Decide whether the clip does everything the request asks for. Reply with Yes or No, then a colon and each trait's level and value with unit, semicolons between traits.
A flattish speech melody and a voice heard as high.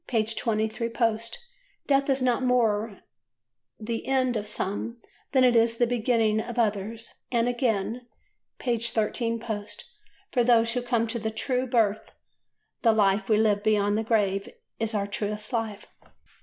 Yes: narrow, 2.1 semitones; high, 225 Hz